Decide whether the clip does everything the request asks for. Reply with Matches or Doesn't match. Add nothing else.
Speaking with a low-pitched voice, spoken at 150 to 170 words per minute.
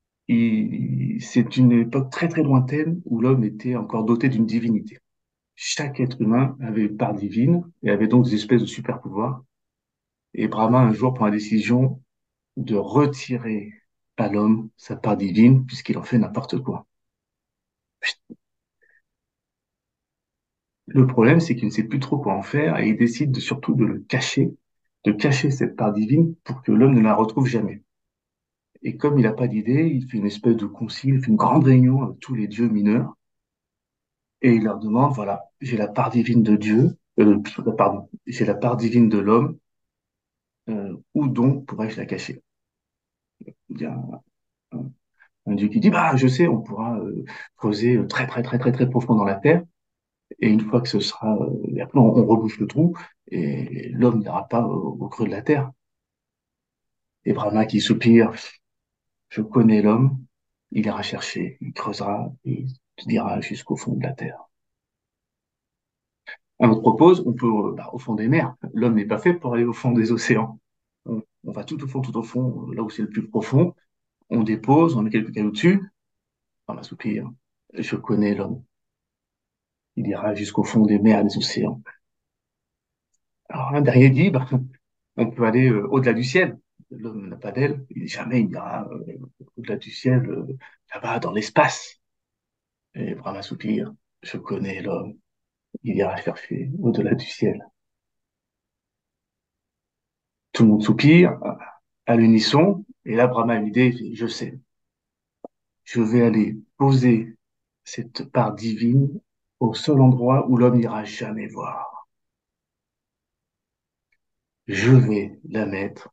Matches